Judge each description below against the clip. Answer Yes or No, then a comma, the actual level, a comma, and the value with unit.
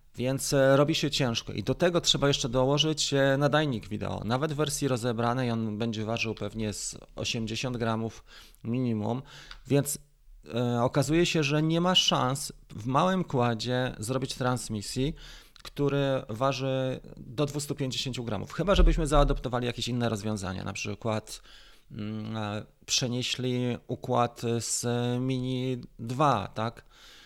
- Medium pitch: No, low, 125 Hz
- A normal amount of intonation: Yes, average, 3.6 semitones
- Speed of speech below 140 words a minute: Yes, average, 125 wpm